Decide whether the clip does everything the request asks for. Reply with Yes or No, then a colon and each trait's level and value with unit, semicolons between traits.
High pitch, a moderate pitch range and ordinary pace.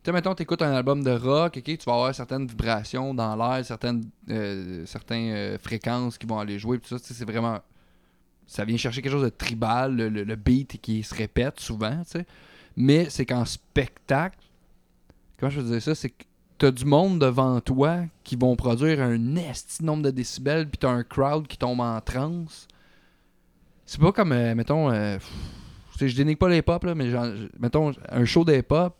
No: low, 125 Hz; average, 4.0 semitones; average, 205 wpm